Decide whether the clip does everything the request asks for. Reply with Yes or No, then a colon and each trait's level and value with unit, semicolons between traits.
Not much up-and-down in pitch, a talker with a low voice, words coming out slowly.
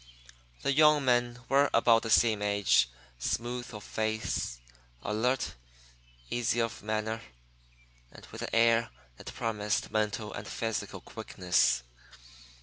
Yes: narrow, 2.3 semitones; low, 115 Hz; slow, 120 wpm